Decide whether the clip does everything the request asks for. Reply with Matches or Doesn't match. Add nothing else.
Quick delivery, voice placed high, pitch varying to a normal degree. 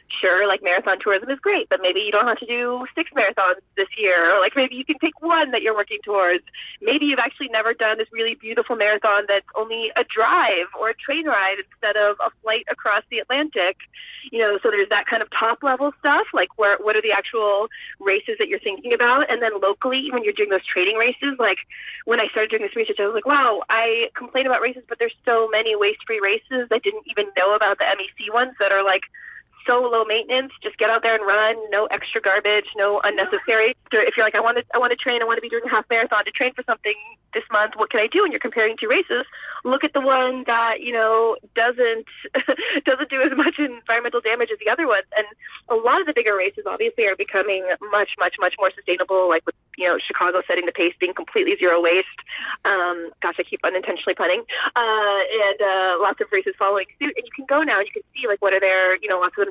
Matches